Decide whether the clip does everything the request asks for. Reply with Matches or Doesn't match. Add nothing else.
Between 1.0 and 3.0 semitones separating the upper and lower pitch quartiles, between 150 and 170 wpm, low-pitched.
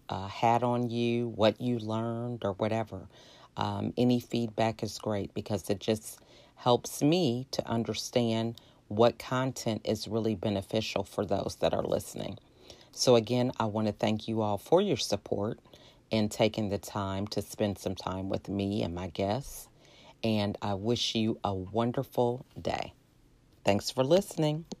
Matches